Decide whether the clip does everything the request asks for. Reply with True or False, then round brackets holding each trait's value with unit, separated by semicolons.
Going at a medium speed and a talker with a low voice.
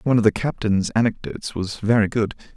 True (190 wpm; 110 Hz)